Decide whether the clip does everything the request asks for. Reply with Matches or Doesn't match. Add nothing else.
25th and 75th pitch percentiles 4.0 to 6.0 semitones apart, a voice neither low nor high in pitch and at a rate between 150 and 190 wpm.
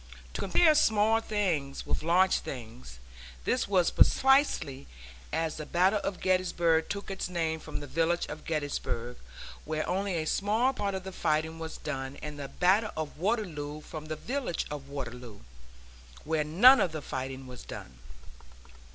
Matches